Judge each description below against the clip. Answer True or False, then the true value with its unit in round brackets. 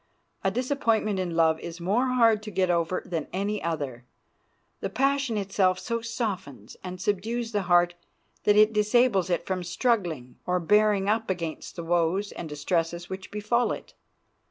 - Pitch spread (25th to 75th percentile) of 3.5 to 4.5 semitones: True (4.1 semitones)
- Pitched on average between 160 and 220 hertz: True (190 Hz)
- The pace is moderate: True (160 wpm)